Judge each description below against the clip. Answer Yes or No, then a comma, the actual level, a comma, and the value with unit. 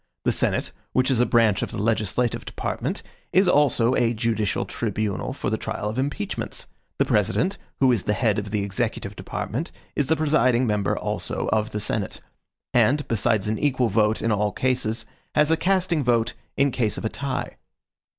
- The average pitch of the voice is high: No, low, 115 Hz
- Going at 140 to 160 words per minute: No, average, 180 wpm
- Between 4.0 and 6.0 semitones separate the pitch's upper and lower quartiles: Yes, average, 4.4 semitones